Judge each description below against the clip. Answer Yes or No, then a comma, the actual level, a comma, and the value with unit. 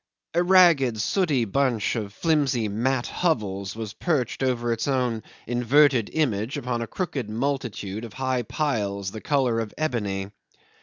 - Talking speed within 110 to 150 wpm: Yes, average, 145 wpm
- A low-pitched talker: Yes, low, 120 Hz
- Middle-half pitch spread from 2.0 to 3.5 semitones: No, average, 4.5 semitones